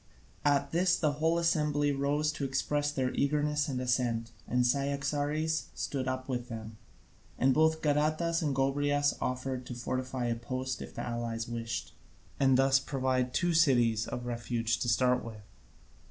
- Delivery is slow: No, average, 155 wpm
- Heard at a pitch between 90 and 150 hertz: Yes, low, 135 Hz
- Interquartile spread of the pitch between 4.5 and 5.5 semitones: No, average, 3.0 semitones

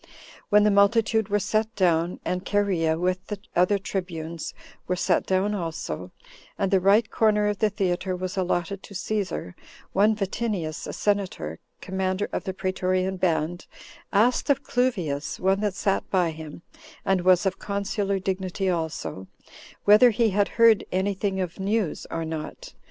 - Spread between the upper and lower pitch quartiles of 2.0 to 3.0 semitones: Yes, narrow, 2.5 semitones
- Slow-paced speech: No, average, 155 wpm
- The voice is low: No, high, 190 Hz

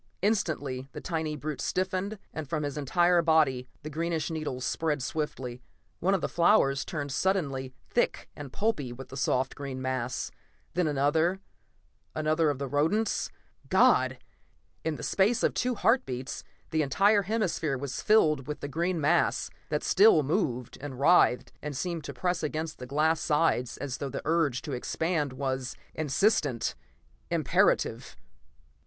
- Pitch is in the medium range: Yes, medium, 150 Hz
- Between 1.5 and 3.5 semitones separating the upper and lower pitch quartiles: No, average, 4.3 semitones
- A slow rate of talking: No, average, 155 wpm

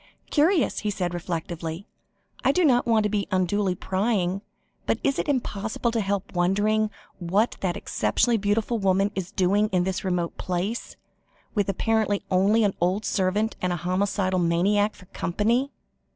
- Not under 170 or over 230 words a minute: No, average, 155 wpm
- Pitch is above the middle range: Yes, high, 200 Hz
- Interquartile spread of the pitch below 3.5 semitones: Yes, average, 3.0 semitones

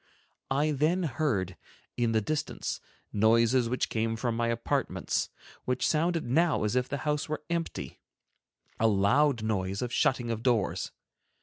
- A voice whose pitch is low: Yes, low, 120 Hz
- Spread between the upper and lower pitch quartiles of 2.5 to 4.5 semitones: No, average, 5.0 semitones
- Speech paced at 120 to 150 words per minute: Yes, average, 145 wpm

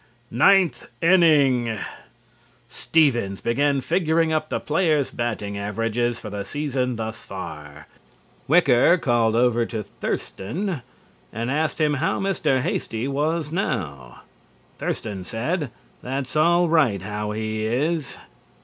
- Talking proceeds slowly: Yes, slow, 115 wpm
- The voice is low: Yes, low, 130 Hz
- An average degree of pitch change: No, wide, 6.0 semitones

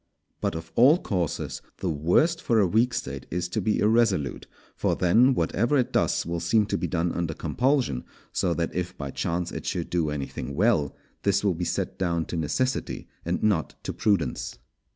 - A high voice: No, very low, 90 Hz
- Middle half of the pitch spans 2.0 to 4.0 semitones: No, wide, 5.4 semitones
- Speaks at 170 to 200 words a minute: Yes, average, 190 wpm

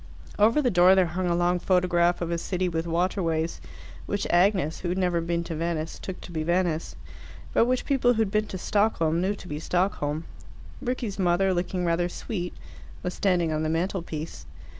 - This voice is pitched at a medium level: Yes, medium, 175 Hz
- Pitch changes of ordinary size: No, narrow, 2.3 semitones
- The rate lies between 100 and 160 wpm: No, average, 190 wpm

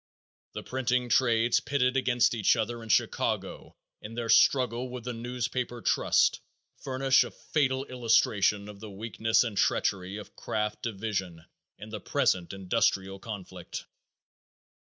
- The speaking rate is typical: No, slow, 130 wpm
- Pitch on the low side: Yes, low, 115 Hz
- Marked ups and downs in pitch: No, average, 3.3 semitones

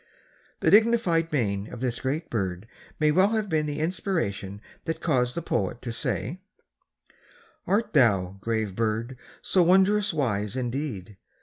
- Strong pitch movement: Yes, wide, 8.0 semitones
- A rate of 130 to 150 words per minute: Yes, average, 140 wpm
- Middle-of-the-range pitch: No, low, 130 Hz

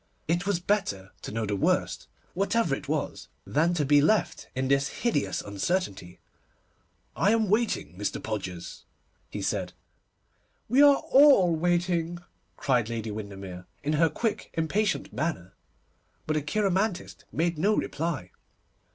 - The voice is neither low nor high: Yes, medium, 160 Hz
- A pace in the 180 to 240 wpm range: No, slow, 135 wpm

